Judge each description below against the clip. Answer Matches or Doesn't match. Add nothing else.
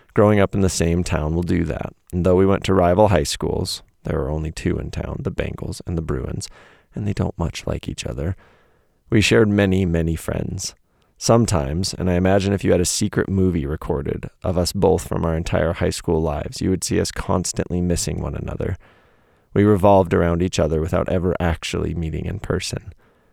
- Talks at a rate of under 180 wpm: Doesn't match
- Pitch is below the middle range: Matches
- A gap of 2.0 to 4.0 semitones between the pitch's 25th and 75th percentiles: Matches